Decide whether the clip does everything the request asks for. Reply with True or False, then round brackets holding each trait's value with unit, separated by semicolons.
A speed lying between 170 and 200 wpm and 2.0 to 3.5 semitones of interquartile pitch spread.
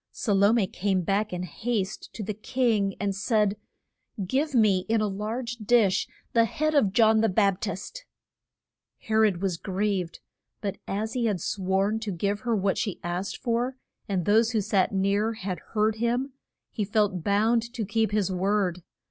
True (175 wpm; 2.6 semitones)